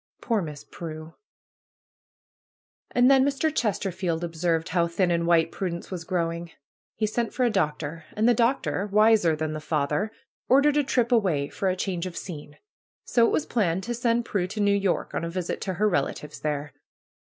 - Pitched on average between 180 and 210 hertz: Yes, medium, 185 Hz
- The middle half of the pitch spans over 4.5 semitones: Yes, average, 5.2 semitones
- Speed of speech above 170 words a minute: Yes, average, 185 wpm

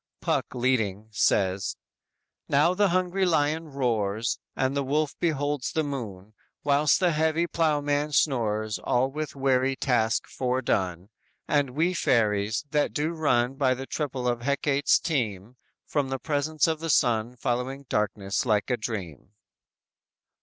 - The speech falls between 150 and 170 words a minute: No, average, 140 wpm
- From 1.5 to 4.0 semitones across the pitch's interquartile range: No, average, 5.0 semitones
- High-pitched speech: No, low, 135 Hz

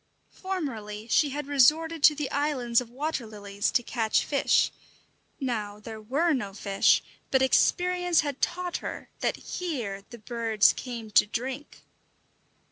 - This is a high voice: Yes, very high, 255 Hz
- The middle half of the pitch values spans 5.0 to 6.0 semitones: Yes, wide, 5.5 semitones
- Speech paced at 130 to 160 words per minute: Yes, average, 140 wpm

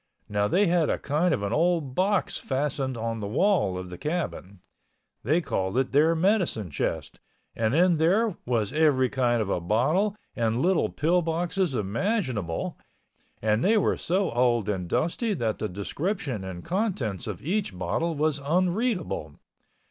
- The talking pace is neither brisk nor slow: Yes, average, 160 wpm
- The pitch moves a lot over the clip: Yes, wide, 8.5 semitones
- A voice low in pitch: No, medium, 145 Hz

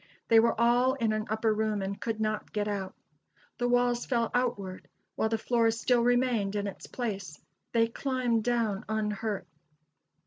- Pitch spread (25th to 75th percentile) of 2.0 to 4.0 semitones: Yes, narrow, 2.4 semitones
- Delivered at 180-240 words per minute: No, average, 165 wpm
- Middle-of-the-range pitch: No, high, 225 Hz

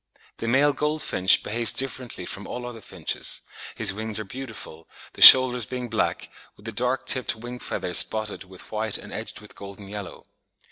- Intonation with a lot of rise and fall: No, average, 3.6 semitones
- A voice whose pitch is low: Yes, low, 115 Hz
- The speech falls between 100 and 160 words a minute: No, average, 175 wpm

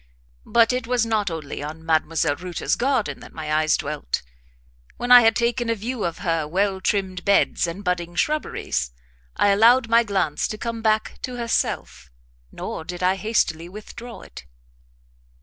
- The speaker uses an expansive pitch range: Yes, wide, 5.8 semitones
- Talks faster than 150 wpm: Yes, average, 165 wpm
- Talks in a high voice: Yes, high, 200 Hz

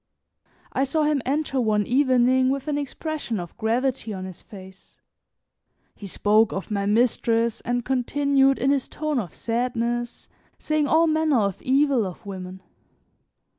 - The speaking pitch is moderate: No, high, 245 Hz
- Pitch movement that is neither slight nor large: Yes, average, 4.6 semitones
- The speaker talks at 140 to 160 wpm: Yes, average, 145 wpm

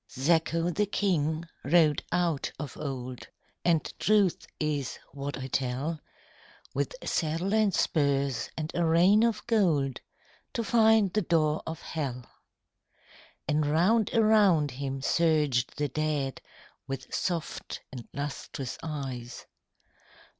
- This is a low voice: No, medium, 155 Hz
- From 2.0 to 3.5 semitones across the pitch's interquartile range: No, average, 4.3 semitones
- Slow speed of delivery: Yes, slow, 120 wpm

